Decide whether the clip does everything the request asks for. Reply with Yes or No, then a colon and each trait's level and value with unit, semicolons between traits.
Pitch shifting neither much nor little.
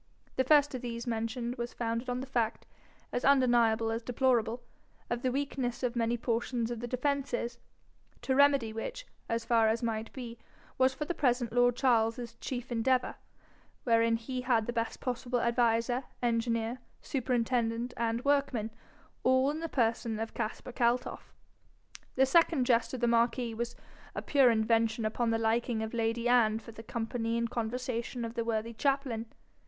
No: narrow, 1.8 semitones